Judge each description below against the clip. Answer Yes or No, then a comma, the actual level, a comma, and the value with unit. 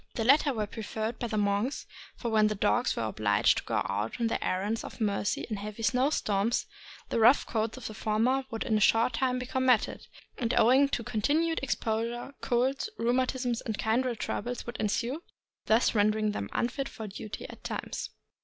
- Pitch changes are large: No, average, 2.9 semitones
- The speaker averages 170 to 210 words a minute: Yes, average, 190 wpm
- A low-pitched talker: No, high, 230 Hz